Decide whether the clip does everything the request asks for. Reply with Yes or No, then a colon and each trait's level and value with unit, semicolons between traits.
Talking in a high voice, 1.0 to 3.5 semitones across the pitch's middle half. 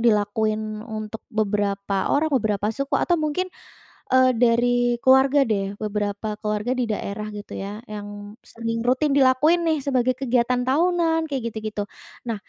No: high, 230 Hz; average, 3.9 semitones